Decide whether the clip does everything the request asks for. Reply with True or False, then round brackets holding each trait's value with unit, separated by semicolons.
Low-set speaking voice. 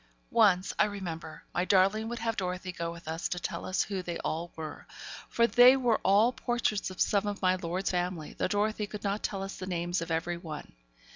False (185 Hz)